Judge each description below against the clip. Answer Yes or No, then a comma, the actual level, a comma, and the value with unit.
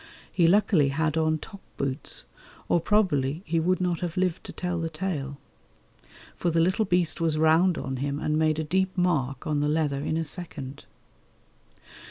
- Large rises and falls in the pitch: No, average, 3.3 semitones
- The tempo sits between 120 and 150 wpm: No, average, 180 wpm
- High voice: No, medium, 160 Hz